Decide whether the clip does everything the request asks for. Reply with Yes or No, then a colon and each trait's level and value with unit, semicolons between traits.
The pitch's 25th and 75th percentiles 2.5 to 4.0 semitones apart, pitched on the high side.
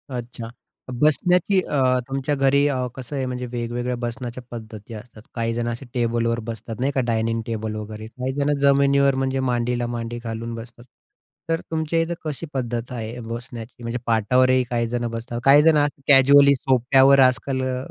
No: average, 2.8 semitones; low, 125 Hz